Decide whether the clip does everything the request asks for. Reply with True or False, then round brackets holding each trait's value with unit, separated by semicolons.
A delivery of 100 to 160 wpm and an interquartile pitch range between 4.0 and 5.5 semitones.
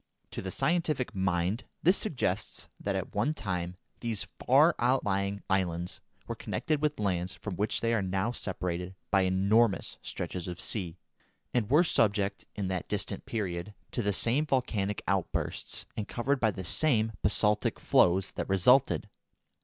True (155 wpm; 4.6 semitones)